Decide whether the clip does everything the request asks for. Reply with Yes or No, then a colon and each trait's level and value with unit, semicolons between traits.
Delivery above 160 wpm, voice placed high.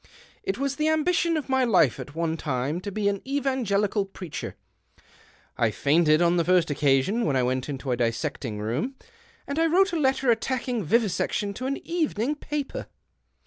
Yes: average, 180 wpm; high, 200 Hz